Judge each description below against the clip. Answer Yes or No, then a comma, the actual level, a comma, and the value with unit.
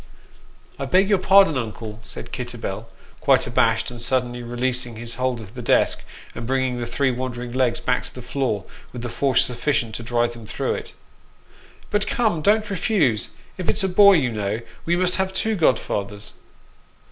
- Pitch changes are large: Yes, wide, 6.7 semitones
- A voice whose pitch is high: No, low, 125 Hz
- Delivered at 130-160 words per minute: No, average, 180 wpm